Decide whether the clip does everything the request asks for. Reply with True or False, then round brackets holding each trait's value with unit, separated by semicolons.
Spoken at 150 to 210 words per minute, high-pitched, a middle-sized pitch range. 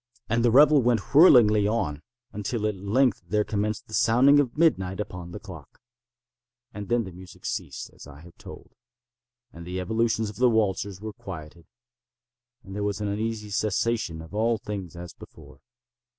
False (170 wpm; 105 Hz; 3.6 semitones)